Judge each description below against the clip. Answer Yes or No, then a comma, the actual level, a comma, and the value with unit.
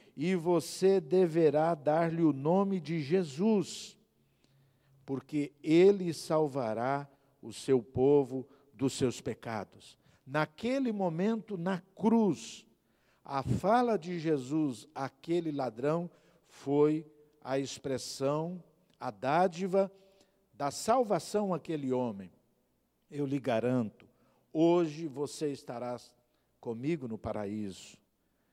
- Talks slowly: Yes, slow, 95 wpm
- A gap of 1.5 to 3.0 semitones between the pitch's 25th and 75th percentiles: No, average, 5.0 semitones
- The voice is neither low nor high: Yes, medium, 155 Hz